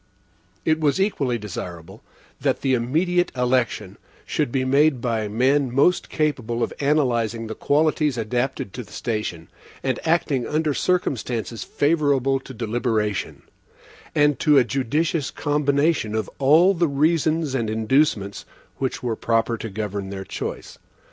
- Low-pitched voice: Yes, low, 130 Hz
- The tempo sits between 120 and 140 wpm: Yes, slow, 135 wpm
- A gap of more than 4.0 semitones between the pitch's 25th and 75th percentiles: Yes, average, 4.8 semitones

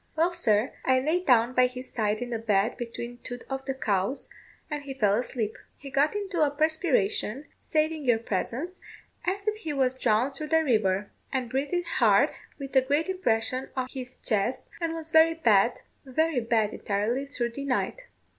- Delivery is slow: No, average, 185 wpm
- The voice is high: Yes, very high, 260 Hz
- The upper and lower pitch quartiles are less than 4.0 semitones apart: No, average, 5.1 semitones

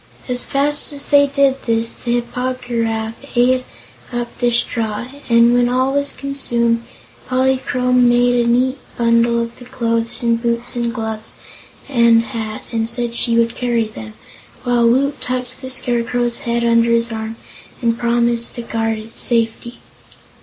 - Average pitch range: No, narrow, 1.4 semitones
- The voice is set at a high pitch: Yes, high, 235 Hz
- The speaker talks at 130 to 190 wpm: Yes, average, 160 wpm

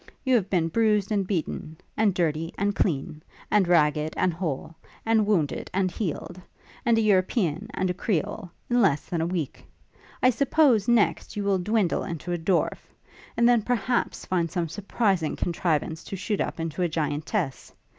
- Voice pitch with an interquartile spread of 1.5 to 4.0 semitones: No, average, 4.4 semitones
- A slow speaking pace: No, average, 170 wpm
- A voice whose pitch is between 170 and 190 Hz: Yes, medium, 185 Hz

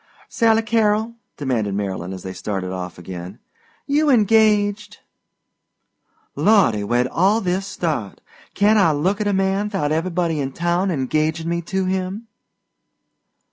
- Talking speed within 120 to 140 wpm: Yes, slow, 135 wpm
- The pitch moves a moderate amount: No, wide, 8.5 semitones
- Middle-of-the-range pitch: Yes, medium, 180 Hz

